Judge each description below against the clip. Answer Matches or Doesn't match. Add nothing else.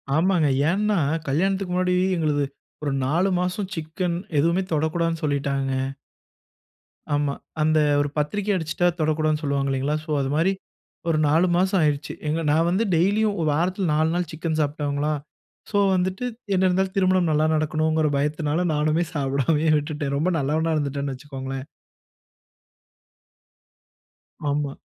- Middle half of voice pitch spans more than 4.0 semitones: Doesn't match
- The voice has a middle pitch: Matches